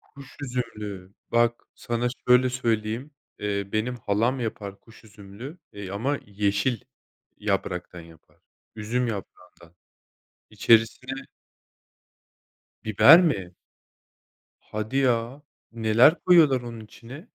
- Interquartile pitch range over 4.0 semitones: No, average, 3.7 semitones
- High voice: No, low, 115 Hz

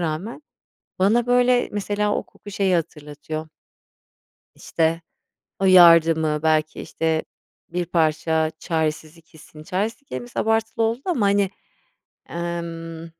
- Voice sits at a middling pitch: Yes, medium, 170 Hz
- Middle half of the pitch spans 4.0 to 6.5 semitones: Yes, average, 4.4 semitones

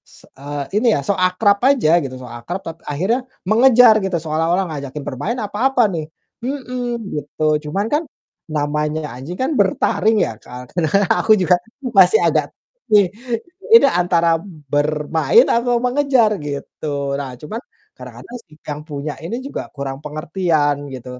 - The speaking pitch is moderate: Yes, medium, 170 Hz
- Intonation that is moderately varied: No, wide, 7.0 semitones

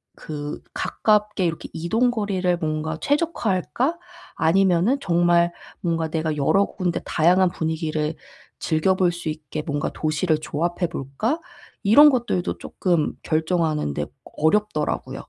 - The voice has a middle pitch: Yes, medium, 170 Hz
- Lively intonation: No, average, 3.9 semitones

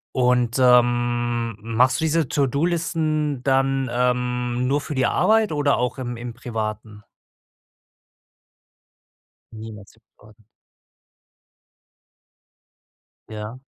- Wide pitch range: No, average, 2.8 semitones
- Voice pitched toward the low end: Yes, low, 125 Hz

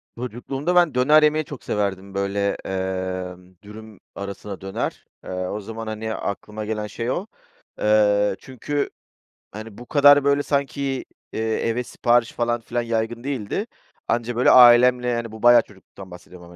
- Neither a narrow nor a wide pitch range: Yes, average, 3.6 semitones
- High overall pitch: No, low, 110 Hz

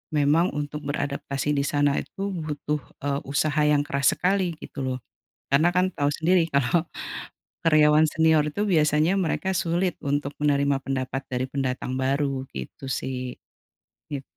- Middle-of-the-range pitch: Yes, medium, 145 Hz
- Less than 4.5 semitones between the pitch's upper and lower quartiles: Yes, narrow, 2.6 semitones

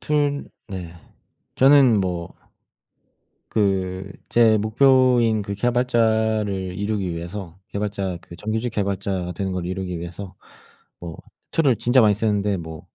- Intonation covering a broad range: No, average, 3.4 semitones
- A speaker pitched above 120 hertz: No, low, 100 Hz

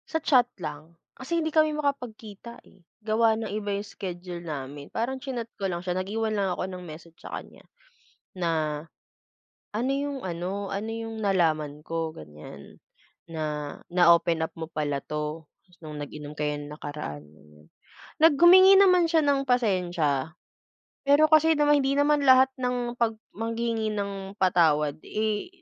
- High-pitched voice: Yes, high, 195 Hz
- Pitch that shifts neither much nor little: No, wide, 7.9 semitones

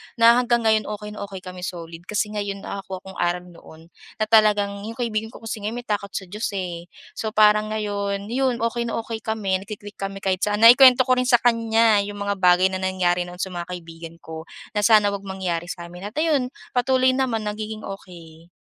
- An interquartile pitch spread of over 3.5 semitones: No, average, 3.1 semitones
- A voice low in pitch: No, high, 205 Hz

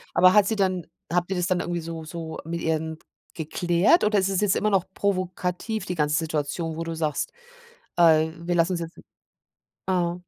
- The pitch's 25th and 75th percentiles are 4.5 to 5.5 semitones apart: No, narrow, 2.4 semitones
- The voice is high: No, medium, 175 Hz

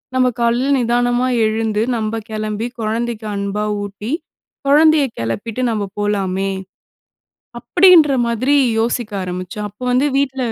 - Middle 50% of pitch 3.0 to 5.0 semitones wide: Yes, average, 3.5 semitones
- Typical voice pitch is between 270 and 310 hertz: No, high, 225 Hz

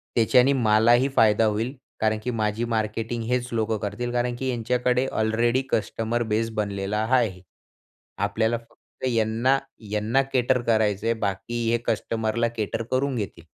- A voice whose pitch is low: Yes, low, 115 Hz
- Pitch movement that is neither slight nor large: No, narrow, 2.1 semitones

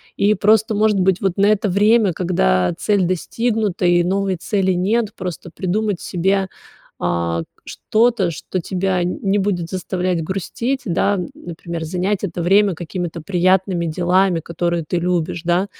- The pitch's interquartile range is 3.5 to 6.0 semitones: No, narrow, 2.5 semitones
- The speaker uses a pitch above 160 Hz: Yes, medium, 185 Hz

